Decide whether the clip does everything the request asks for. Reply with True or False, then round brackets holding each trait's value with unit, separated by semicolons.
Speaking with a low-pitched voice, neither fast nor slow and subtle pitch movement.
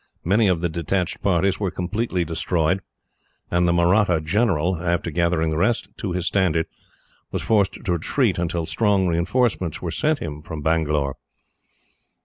False (85 Hz; 150 wpm; 3.1 semitones)